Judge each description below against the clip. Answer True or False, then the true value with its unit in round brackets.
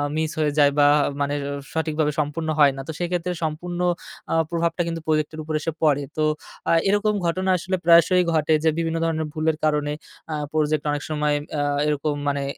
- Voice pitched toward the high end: False (155 Hz)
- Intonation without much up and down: True (2.0 semitones)